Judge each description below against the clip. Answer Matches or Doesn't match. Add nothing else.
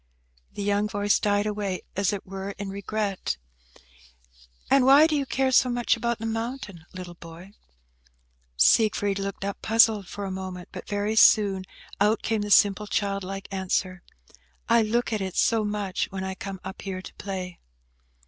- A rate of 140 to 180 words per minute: Matches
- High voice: Matches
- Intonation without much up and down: Matches